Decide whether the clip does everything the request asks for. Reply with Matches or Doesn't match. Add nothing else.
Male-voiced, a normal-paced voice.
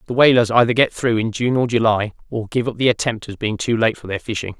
Doesn't match